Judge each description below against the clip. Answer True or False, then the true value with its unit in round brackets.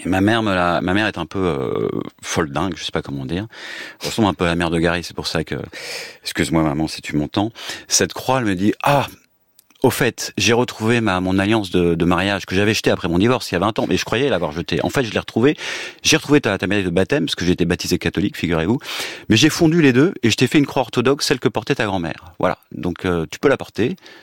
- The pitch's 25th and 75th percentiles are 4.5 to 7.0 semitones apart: True (5.0 semitones)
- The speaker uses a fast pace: True (270 wpm)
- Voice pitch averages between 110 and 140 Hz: False (100 Hz)